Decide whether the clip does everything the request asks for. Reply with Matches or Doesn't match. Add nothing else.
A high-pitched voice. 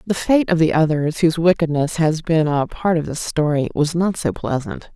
Doesn't match